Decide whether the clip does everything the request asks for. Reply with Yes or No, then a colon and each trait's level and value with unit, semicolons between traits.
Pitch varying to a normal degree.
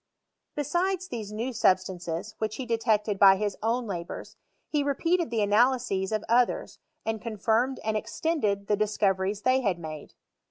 Yes: average, 4.1 semitones